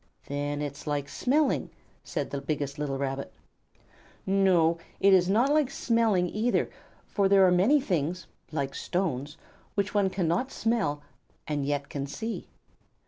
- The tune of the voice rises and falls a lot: Yes, wide, 6.0 semitones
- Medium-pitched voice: Yes, medium, 175 Hz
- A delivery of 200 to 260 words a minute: No, average, 145 wpm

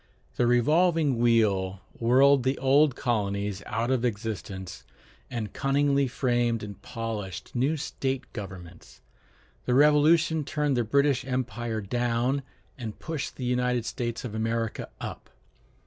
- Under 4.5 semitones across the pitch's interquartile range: Yes, average, 3.7 semitones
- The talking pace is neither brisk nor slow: No, slow, 125 wpm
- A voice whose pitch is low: Yes, low, 120 Hz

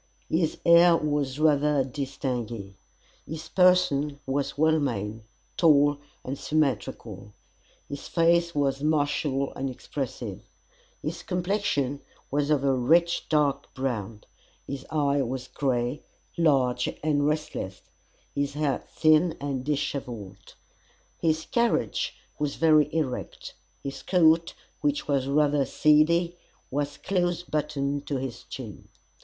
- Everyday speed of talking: No, slow, 115 wpm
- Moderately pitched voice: Yes, medium, 145 Hz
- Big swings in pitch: No, average, 2.9 semitones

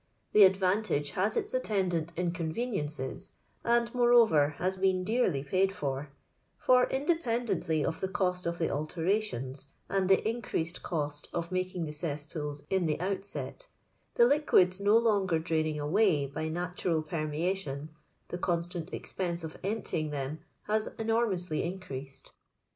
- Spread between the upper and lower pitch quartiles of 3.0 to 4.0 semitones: No, average, 4.5 semitones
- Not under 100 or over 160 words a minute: Yes, average, 140 wpm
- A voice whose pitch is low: No, medium, 180 Hz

